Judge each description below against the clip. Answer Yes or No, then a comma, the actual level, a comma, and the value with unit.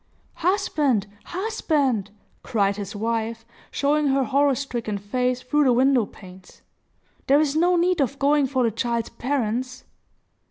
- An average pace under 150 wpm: Yes, slow, 135 wpm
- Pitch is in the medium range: No, very high, 255 Hz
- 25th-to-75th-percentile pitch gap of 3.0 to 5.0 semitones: Yes, average, 4.2 semitones